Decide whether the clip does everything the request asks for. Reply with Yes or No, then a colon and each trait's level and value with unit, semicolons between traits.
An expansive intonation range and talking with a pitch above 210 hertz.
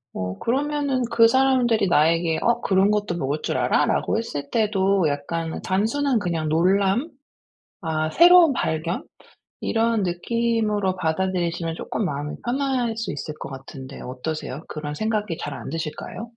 No: wide, 6.5 semitones; high, 190 Hz